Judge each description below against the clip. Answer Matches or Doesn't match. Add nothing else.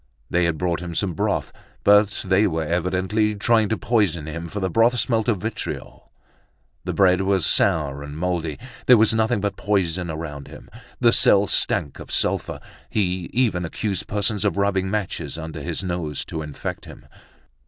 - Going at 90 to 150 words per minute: Doesn't match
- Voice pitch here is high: Doesn't match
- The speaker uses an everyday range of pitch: Matches